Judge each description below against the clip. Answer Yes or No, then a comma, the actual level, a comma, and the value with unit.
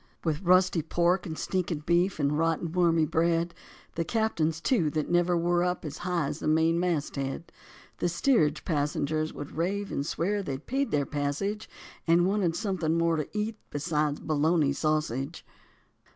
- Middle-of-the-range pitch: Yes, medium, 165 Hz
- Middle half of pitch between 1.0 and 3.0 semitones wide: Yes, average, 2.7 semitones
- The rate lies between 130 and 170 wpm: Yes, average, 165 wpm